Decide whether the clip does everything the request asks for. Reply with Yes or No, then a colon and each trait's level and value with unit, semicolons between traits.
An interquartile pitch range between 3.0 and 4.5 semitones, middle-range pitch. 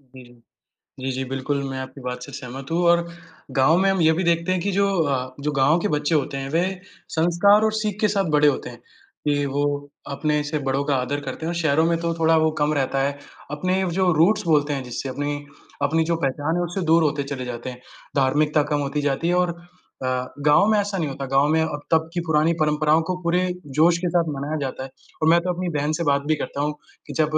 Yes: average, 3.7 semitones; medium, 150 Hz